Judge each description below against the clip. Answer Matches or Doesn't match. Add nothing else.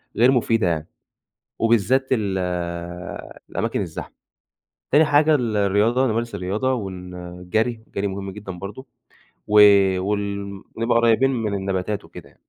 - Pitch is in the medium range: Doesn't match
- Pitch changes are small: Doesn't match